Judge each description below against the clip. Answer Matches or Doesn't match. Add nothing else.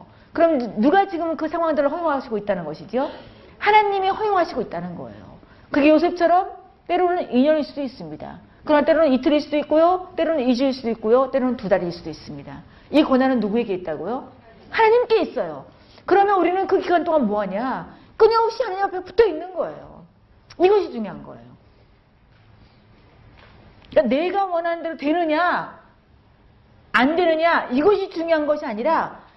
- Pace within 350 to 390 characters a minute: Matches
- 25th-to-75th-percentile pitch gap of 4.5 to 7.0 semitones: Doesn't match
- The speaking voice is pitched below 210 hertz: Doesn't match